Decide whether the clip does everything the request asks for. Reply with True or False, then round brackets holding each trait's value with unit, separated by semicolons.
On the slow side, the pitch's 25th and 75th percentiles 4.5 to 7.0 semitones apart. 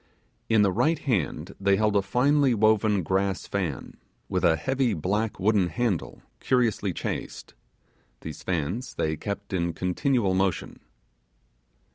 False (130 wpm; 3.7 semitones)